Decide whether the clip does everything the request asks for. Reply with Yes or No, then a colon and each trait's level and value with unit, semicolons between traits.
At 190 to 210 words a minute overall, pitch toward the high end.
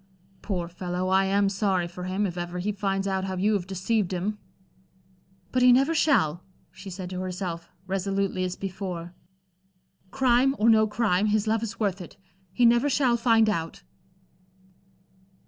No: average, 165 wpm; high, 195 Hz